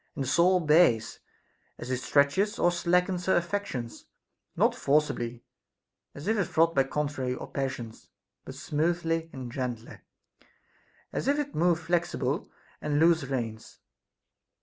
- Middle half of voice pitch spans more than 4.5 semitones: Yes, average, 5.1 semitones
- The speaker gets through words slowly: Yes, slow, 130 wpm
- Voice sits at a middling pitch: Yes, medium, 150 Hz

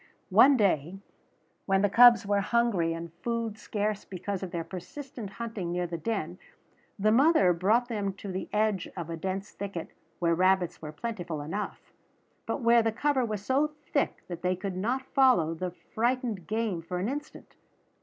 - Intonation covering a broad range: No, average, 4.7 semitones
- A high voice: Yes, high, 200 Hz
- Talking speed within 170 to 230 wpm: Yes, average, 175 wpm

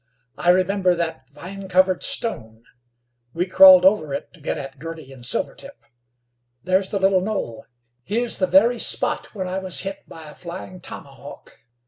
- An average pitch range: Yes, average, 4.1 semitones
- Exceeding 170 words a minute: No, average, 160 wpm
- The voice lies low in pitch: No, medium, 185 Hz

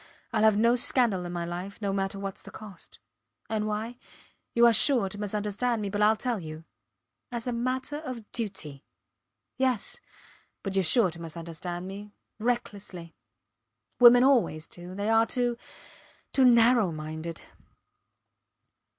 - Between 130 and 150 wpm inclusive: Yes, average, 145 wpm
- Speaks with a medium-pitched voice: No, high, 210 Hz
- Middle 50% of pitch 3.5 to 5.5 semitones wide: Yes, average, 4.7 semitones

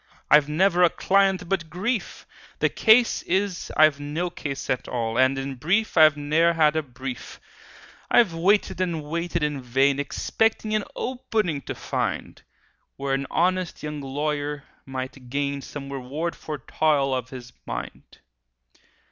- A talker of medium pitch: Yes, medium, 150 Hz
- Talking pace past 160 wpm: No, average, 150 wpm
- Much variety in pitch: No, average, 4.5 semitones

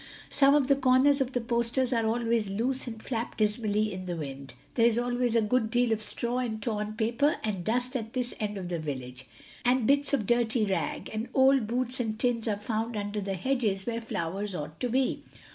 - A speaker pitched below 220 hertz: No, high, 230 Hz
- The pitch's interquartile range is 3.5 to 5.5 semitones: No, average, 3.1 semitones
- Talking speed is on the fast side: Yes, fast, 210 wpm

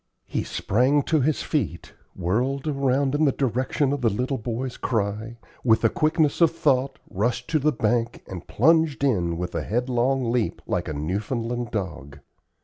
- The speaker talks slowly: No, average, 165 wpm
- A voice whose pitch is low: Yes, low, 125 Hz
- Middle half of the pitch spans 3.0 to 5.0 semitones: Yes, average, 4.5 semitones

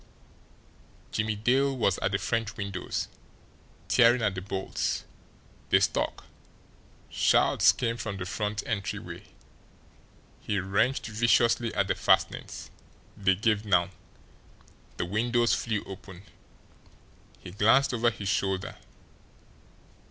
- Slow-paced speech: Yes, slow, 110 wpm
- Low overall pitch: Yes, low, 105 Hz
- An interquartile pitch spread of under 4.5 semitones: Yes, average, 3.2 semitones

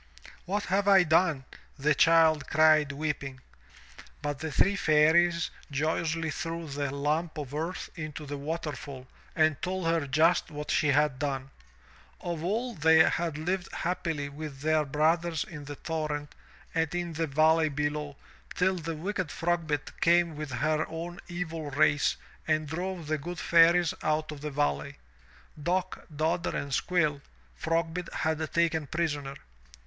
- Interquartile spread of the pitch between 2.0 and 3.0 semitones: Yes, narrow, 2.4 semitones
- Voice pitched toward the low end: No, medium, 155 Hz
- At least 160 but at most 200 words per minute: No, average, 145 wpm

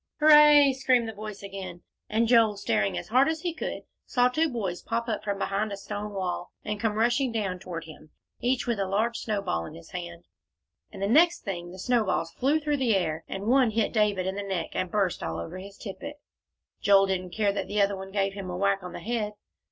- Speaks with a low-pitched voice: No, high, 205 Hz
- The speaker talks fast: Yes, fast, 225 wpm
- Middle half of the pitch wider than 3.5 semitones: Yes, average, 3.9 semitones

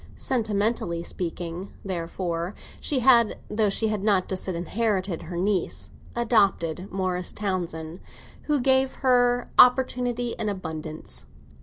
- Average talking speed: No, slow, 110 wpm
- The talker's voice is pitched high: Yes, high, 200 Hz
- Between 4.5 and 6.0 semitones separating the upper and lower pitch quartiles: Yes, average, 5.2 semitones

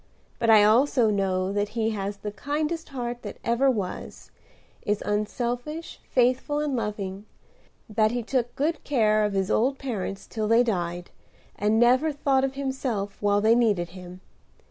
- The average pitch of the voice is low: No, high, 225 Hz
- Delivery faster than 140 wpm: Yes, average, 160 wpm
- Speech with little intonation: No, average, 4.3 semitones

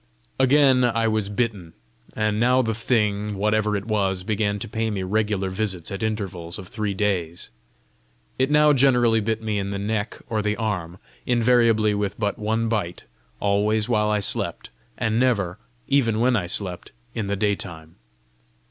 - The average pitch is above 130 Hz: No, low, 105 Hz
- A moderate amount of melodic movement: No, narrow, 2.2 semitones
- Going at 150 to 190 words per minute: Yes, average, 165 wpm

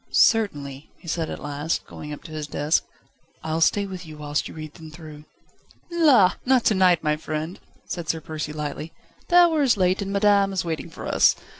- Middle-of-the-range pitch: Yes, medium, 165 Hz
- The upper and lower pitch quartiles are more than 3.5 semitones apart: Yes, average, 4.6 semitones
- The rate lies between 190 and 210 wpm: Yes, average, 200 wpm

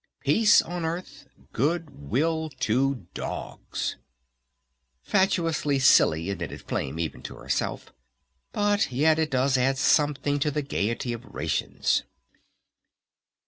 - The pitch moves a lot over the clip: No, average, 4.5 semitones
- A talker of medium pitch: Yes, medium, 145 Hz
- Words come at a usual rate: No, slow, 110 wpm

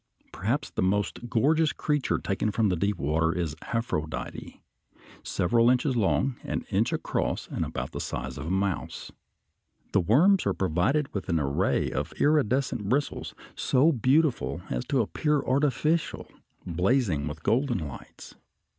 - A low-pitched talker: Yes, low, 115 Hz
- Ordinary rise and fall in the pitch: No, wide, 7.7 semitones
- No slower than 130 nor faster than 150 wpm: Yes, average, 140 wpm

